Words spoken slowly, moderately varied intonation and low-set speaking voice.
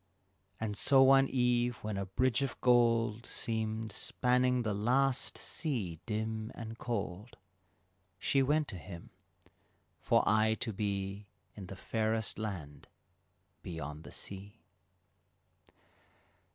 Yes: slow, 115 wpm; average, 3.6 semitones; low, 110 Hz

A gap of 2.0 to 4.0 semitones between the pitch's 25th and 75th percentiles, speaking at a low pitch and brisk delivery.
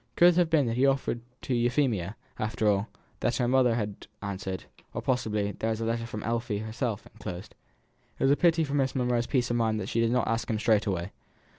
Yes: average, 3.0 semitones; low, 115 Hz; fast, 240 wpm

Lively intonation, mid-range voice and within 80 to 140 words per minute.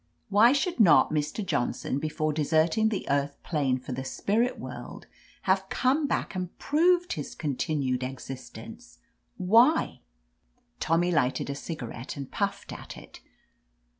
Yes: wide, 7.7 semitones; medium, 160 Hz; slow, 135 wpm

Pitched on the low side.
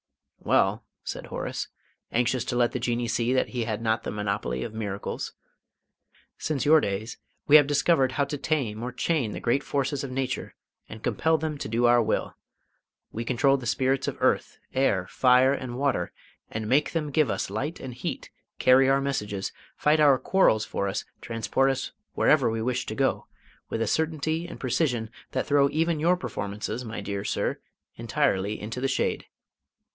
Yes: low, 125 Hz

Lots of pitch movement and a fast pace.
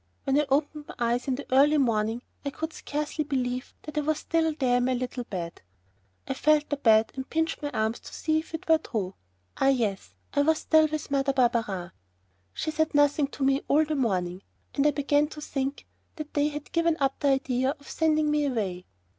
No: average, 3.5 semitones; fast, 215 wpm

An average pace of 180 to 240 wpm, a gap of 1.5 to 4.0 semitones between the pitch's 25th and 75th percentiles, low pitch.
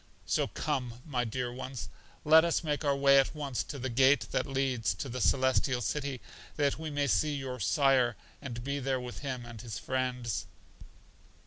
Yes: average, 185 wpm; narrow, 2.4 semitones; low, 130 Hz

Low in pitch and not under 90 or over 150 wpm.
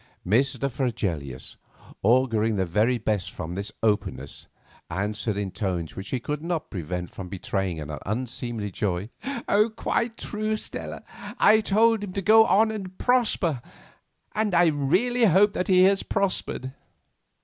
Yes: low, 120 Hz; average, 140 wpm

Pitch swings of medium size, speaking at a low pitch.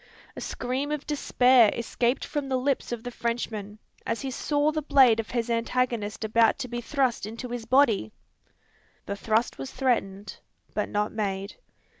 No: average, 3.2 semitones; high, 235 Hz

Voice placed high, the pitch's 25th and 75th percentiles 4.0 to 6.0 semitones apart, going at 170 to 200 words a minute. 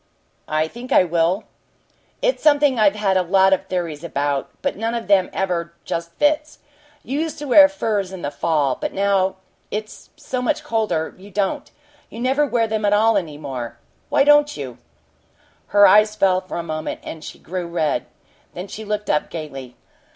Yes: high, 195 Hz; average, 5.2 semitones; average, 185 wpm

